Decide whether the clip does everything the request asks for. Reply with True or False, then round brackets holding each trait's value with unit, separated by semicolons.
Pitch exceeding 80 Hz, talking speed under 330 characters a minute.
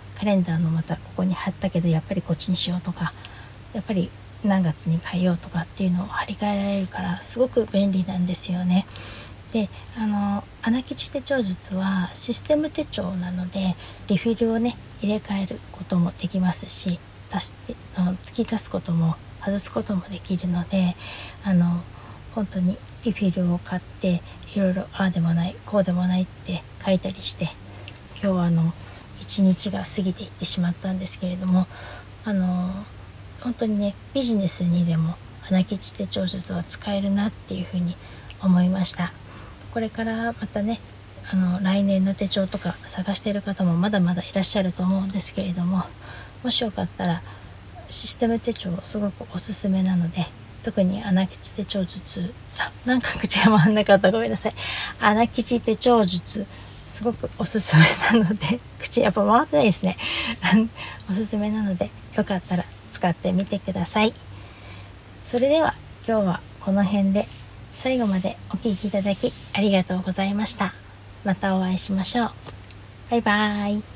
True (190 Hz; 320 characters per minute)